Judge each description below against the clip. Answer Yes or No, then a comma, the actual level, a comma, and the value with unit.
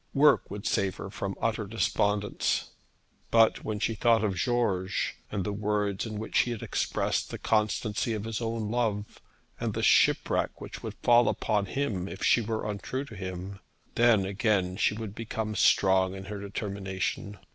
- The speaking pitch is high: No, low, 105 Hz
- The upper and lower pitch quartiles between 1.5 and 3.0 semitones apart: Yes, narrow, 2.4 semitones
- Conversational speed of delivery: Yes, average, 170 wpm